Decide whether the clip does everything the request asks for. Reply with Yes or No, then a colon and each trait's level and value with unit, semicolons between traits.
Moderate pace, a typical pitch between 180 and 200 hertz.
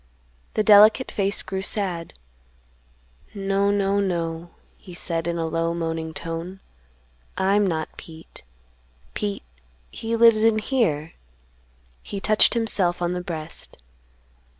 No: slow, 120 wpm; high, 190 Hz